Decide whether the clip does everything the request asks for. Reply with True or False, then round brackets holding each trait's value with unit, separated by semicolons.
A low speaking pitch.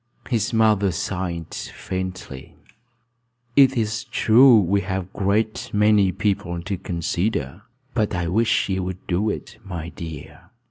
True (95 Hz)